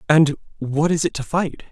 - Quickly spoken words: Yes, fast, 210 wpm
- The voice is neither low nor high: Yes, medium, 150 Hz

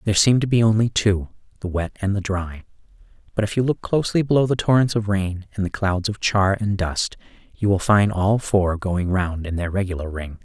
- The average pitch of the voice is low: Yes, low, 100 Hz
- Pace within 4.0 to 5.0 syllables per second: No, 5.4 syllables/s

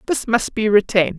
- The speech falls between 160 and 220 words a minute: Yes, average, 200 wpm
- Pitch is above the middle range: Yes, high, 215 Hz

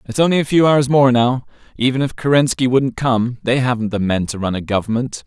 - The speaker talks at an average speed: No, fast, 230 wpm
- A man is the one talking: Yes, male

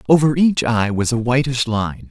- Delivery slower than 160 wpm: No, average, 200 wpm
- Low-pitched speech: Yes, low, 125 Hz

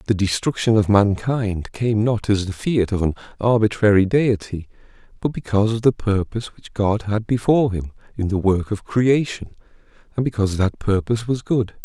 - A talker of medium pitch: No, low, 105 Hz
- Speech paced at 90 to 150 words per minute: No, average, 170 wpm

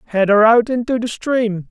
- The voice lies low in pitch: No, high, 225 Hz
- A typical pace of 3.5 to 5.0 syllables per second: Yes, 4.9 syllables/s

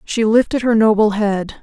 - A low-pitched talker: No, high, 215 Hz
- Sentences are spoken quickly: No, average, 185 wpm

